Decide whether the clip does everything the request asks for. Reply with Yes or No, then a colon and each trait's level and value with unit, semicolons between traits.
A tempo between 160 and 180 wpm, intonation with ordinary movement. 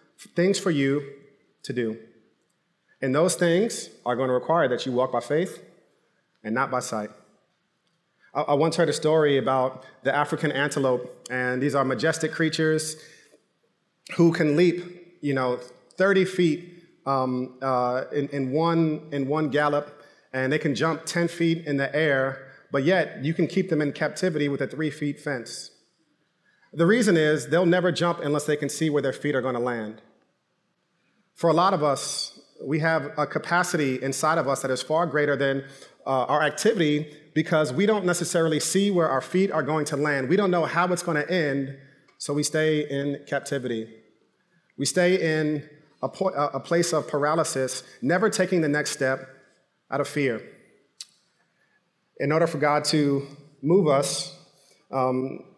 Yes: average, 170 wpm; average, 3.4 semitones